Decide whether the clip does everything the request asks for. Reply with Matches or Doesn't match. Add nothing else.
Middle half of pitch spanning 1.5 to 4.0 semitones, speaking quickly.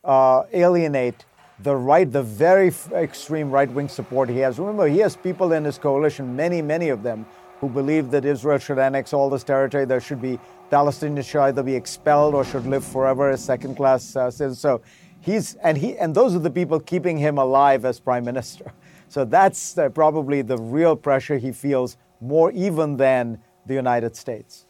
Doesn't match